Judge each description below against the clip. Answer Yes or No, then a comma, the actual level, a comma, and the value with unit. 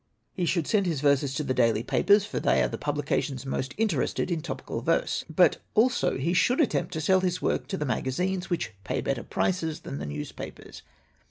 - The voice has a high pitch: No, medium, 160 Hz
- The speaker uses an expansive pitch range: Yes, wide, 6.0 semitones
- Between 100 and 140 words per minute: No, average, 200 wpm